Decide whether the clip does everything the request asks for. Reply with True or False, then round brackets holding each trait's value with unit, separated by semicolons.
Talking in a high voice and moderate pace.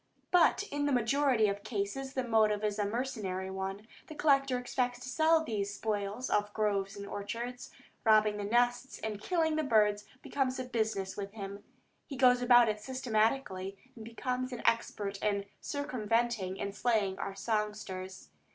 True (220 Hz; 160 wpm)